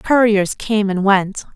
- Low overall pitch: No, high, 205 Hz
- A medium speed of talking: Yes, average, 155 wpm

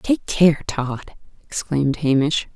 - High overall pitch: No, medium, 150 Hz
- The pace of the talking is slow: Yes, slow, 115 wpm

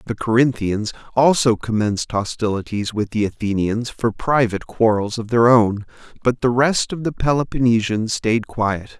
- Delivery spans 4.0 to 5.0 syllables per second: Yes, 4.7 syllables/s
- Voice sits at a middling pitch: No, low, 115 Hz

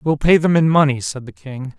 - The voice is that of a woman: No, male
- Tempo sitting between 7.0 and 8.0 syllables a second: No, 5.2 syllables/s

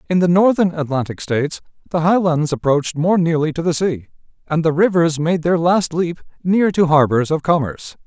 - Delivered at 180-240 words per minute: Yes, average, 185 wpm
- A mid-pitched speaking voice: Yes, medium, 160 Hz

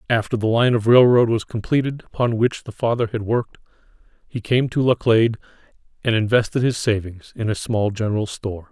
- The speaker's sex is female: No, male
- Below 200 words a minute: Yes, average, 180 wpm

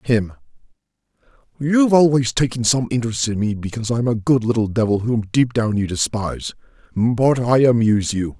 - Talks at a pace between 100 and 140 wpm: No, average, 155 wpm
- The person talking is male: Yes, male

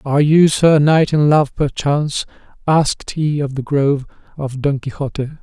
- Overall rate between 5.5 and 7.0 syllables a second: No, 4.9 syllables/s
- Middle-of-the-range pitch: Yes, medium, 145 Hz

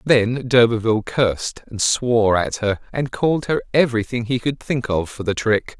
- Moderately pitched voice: No, low, 120 Hz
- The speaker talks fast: No, average, 185 wpm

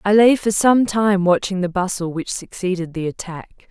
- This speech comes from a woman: Yes, female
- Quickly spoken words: No, average, 195 wpm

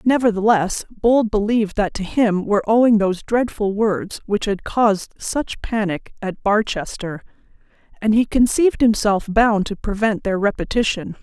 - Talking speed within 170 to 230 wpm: No, average, 140 wpm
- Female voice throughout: Yes, female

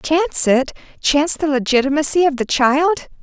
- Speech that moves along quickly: No, average, 150 wpm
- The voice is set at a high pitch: Yes, very high, 290 Hz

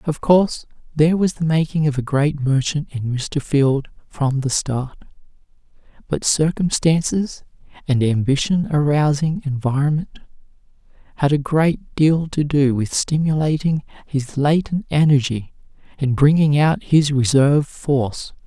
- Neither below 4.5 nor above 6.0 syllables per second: No, 4.3 syllables/s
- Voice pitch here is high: No, medium, 145 Hz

